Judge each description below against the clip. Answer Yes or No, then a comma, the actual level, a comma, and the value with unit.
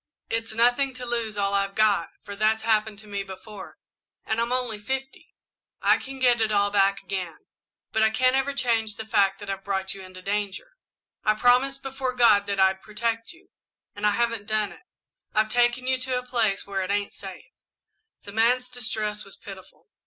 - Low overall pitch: No, high, 220 Hz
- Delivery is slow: No, average, 195 wpm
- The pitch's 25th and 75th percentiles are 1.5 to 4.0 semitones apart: Yes, average, 3.5 semitones